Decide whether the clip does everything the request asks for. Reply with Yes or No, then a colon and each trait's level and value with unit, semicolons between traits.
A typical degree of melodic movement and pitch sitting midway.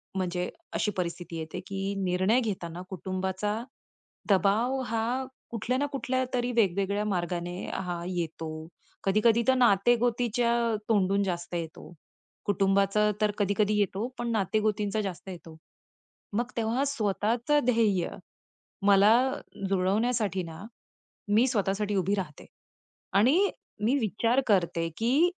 No: average, 4.0 semitones; high, 205 Hz